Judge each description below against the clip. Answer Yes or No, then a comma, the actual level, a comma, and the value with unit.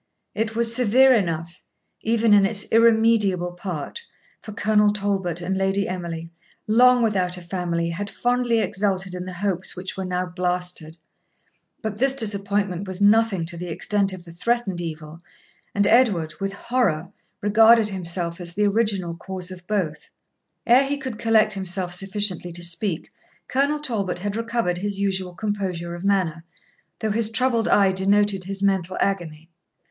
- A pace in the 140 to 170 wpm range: Yes, average, 155 wpm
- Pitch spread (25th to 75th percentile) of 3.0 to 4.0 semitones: Yes, average, 3.5 semitones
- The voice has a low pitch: No, high, 195 Hz